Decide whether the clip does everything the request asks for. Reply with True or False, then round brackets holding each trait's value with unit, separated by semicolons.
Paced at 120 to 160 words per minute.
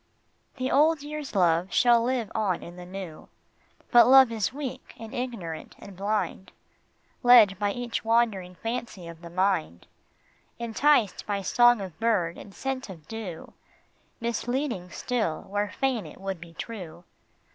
True (145 wpm)